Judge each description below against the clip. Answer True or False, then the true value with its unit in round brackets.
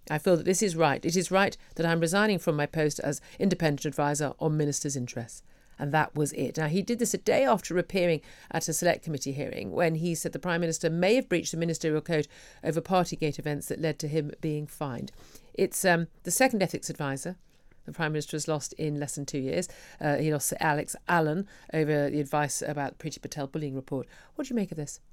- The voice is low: False (155 Hz)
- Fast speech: True (230 wpm)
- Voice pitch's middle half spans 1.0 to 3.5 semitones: True (2.8 semitones)